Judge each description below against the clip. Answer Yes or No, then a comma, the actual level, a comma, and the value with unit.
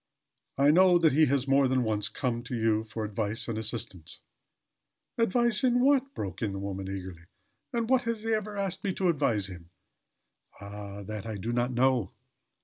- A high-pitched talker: No, low, 120 Hz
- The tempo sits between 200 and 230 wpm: No, average, 190 wpm